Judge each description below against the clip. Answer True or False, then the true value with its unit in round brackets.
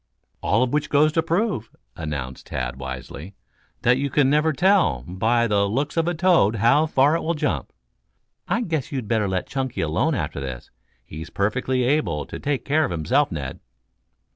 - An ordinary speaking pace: True (180 wpm)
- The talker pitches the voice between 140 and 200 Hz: False (125 Hz)